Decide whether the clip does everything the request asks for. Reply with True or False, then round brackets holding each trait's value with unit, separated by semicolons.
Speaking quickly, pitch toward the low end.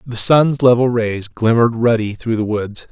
False (185 wpm; 115 Hz)